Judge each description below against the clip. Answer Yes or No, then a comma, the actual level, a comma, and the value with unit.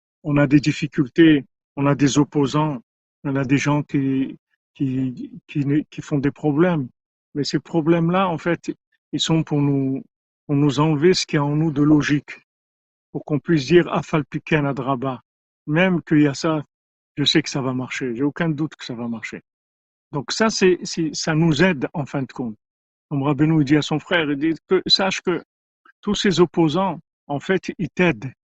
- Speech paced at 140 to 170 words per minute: No, average, 195 wpm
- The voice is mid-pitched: Yes, medium, 150 Hz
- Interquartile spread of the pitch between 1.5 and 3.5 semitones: Yes, average, 2.9 semitones